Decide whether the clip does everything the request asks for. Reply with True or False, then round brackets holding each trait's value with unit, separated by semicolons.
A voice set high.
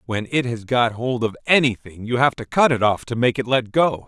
False (120 Hz)